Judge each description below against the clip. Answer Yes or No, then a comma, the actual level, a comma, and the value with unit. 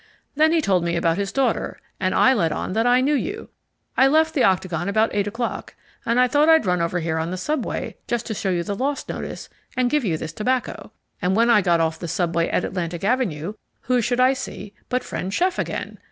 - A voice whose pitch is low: No, high, 210 Hz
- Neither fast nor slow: No, fast, 230 wpm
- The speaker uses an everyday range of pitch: No, wide, 6.4 semitones